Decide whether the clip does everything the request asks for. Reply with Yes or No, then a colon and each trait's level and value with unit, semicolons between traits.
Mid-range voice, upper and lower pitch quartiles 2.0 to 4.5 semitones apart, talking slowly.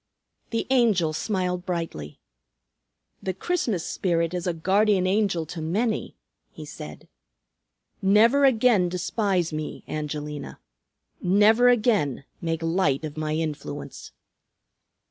No: medium, 180 Hz; average, 5.0 semitones; slow, 105 wpm